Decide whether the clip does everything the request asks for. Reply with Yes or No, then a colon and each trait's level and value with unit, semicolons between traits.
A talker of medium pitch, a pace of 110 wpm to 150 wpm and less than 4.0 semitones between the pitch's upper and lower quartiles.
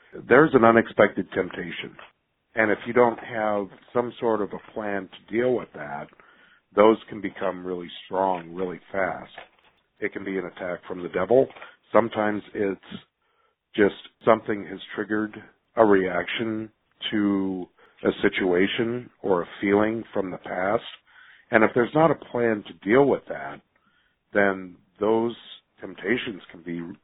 No: low, 105 Hz; average, 145 wpm; average, 3.0 semitones